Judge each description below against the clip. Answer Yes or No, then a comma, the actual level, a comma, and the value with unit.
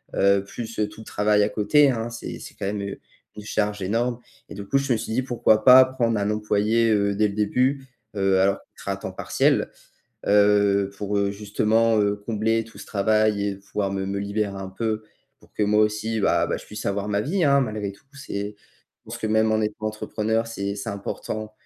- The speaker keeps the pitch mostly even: Yes, narrow, 1.8 semitones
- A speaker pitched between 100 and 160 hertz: Yes, low, 105 Hz